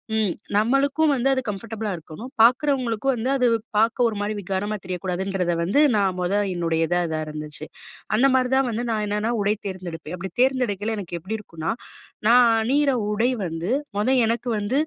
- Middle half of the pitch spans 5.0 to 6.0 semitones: Yes, average, 5.3 semitones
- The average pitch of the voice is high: Yes, high, 210 Hz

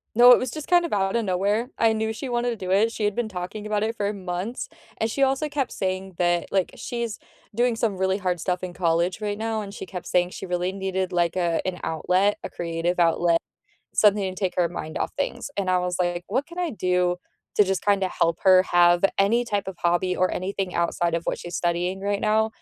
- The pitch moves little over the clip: No, average, 3.6 semitones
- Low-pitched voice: No, high, 190 Hz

